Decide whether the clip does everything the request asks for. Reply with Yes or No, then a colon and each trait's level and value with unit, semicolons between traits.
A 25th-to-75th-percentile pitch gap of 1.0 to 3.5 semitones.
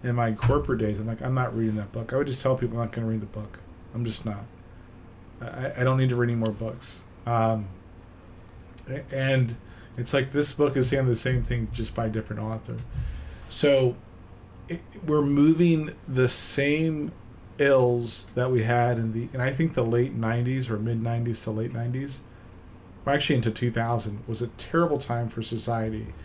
Yes: average, 2.9 semitones